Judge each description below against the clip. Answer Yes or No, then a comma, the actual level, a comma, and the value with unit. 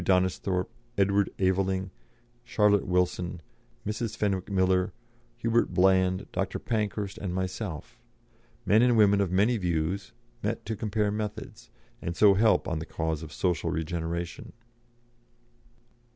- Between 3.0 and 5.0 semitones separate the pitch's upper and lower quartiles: No, narrow, 2.6 semitones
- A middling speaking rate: No, slow, 125 wpm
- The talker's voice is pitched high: No, very low, 95 Hz